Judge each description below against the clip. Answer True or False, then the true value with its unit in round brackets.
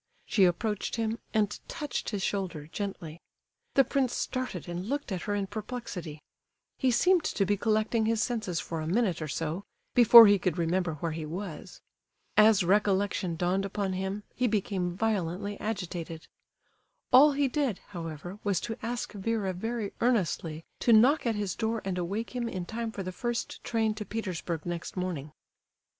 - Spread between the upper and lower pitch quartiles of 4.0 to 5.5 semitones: True (4.3 semitones)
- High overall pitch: True (200 Hz)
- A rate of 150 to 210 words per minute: True (170 wpm)